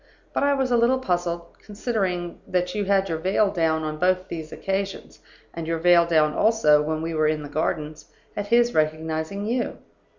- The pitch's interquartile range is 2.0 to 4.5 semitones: Yes, average, 4.2 semitones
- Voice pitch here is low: No, medium, 175 Hz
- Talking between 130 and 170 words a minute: No, average, 190 wpm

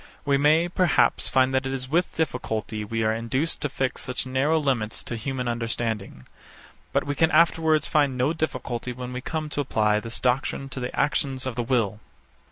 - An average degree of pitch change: Yes, average, 3.7 semitones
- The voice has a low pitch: Yes, low, 130 Hz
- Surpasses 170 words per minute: Yes, average, 190 wpm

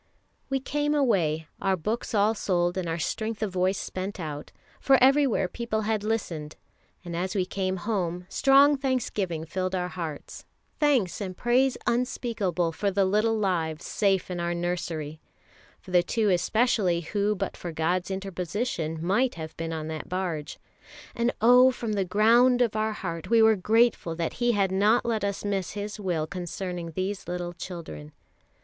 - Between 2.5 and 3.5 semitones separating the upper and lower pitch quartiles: No, average, 4.4 semitones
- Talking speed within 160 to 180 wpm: Yes, average, 170 wpm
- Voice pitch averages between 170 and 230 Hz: Yes, high, 190 Hz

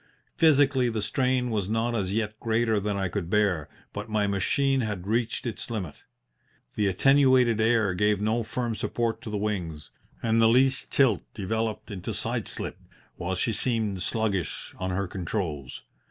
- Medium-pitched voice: No, low, 110 Hz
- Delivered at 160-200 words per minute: Yes, average, 165 wpm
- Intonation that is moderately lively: Yes, average, 3.2 semitones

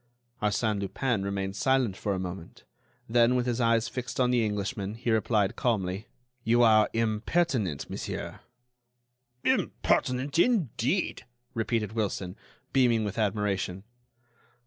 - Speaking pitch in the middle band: No, low, 110 Hz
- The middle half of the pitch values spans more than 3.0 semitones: Yes, average, 3.6 semitones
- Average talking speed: No, slow, 120 wpm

